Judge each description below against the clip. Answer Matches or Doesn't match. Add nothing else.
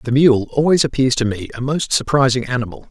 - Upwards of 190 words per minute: Matches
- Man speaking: Matches